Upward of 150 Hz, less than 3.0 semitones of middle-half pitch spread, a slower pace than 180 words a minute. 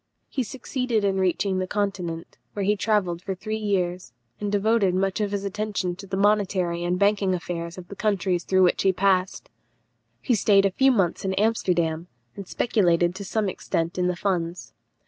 No: high, 190 Hz; narrow, 2.5 semitones; average, 185 wpm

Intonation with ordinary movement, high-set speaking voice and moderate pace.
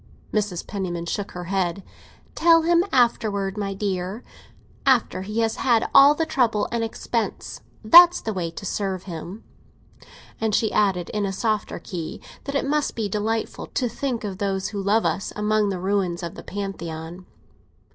Yes: average, 3.2 semitones; high, 205 Hz; average, 170 wpm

